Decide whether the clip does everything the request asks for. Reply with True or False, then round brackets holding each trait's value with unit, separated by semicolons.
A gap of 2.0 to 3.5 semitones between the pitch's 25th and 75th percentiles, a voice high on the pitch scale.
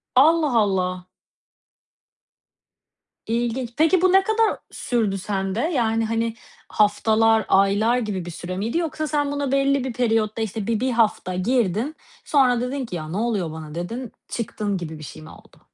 False (5.0 semitones; 225 Hz)